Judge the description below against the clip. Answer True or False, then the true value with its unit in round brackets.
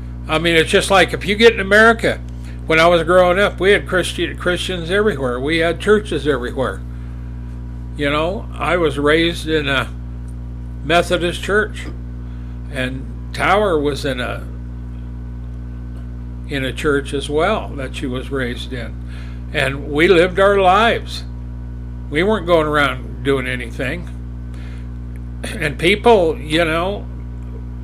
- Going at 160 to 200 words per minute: False (135 wpm)